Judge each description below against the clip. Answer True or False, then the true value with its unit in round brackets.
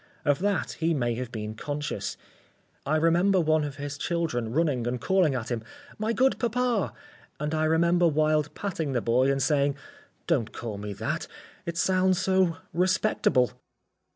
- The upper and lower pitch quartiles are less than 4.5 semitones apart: False (5.5 semitones)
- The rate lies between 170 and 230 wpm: False (160 wpm)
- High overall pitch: False (155 Hz)